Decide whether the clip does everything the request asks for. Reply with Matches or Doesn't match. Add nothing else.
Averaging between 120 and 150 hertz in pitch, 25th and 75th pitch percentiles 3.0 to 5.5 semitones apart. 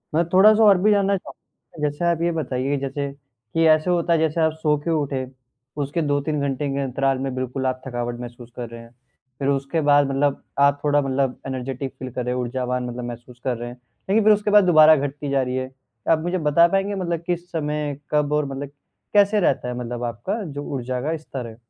Matches